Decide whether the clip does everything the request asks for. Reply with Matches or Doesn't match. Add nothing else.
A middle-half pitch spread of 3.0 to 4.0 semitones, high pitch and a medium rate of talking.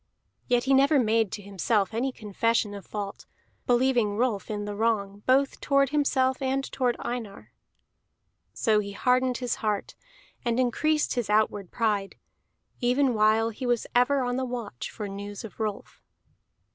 Matches